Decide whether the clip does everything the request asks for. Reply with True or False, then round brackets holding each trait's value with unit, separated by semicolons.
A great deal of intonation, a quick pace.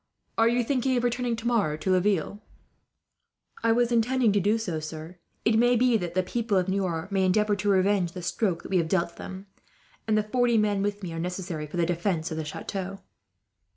False (4.3 semitones; 210 wpm)